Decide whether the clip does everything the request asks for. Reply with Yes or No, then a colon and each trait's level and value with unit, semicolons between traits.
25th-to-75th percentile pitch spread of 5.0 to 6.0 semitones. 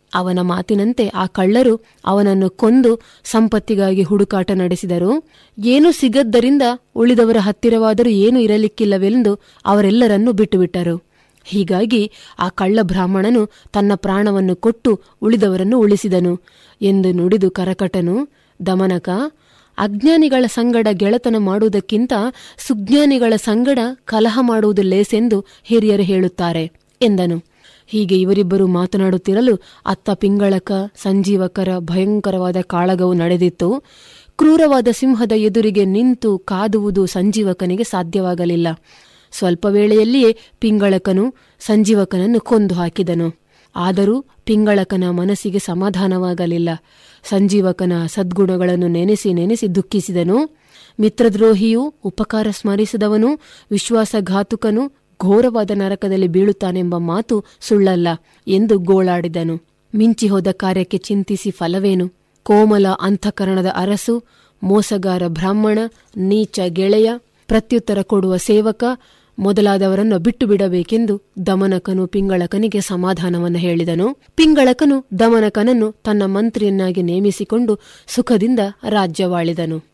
No: average, 3.0 semitones